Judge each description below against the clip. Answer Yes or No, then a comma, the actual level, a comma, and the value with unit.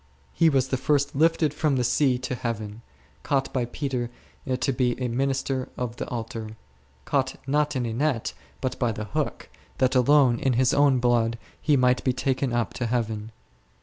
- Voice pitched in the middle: No, low, 125 Hz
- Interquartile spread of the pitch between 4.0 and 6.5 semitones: No, narrow, 2.4 semitones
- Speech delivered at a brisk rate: No, average, 180 wpm